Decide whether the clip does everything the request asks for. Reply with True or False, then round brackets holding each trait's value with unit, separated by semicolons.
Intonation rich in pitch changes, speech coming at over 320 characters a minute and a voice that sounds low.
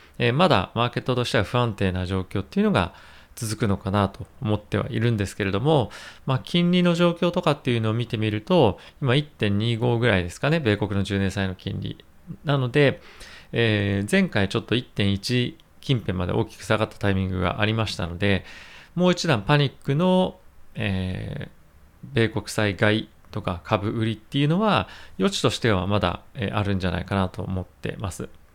False (4.8 semitones; 340 characters per minute; 105 Hz)